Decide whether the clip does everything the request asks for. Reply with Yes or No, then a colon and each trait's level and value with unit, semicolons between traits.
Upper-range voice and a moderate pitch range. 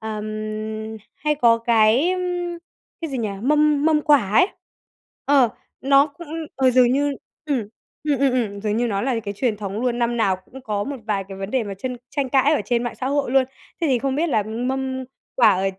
Yes: very high, 255 Hz; average, 4.5 semitones